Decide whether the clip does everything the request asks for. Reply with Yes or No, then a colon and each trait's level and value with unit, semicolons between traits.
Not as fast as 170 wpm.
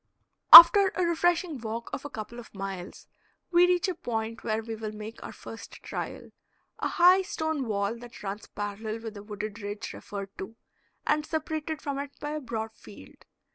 No: average, 180 wpm